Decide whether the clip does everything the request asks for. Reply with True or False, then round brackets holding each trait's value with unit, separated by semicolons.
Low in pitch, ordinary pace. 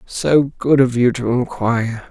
True (125 Hz; 170 wpm)